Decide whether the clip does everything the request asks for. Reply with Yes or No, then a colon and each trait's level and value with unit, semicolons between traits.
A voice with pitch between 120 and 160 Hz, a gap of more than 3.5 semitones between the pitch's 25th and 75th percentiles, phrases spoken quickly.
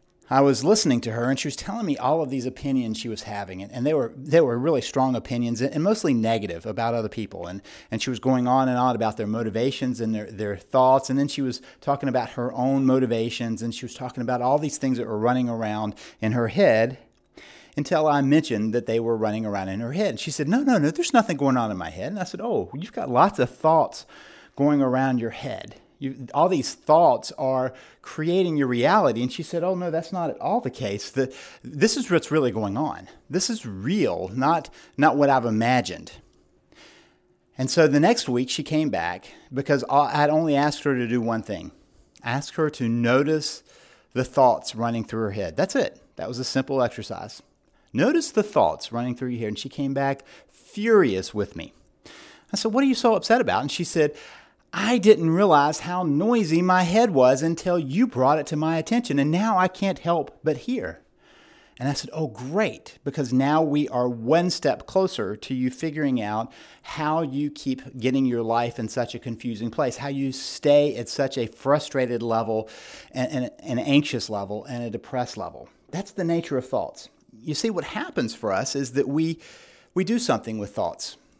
Yes: low, 135 Hz; average, 5.0 semitones; fast, 210 wpm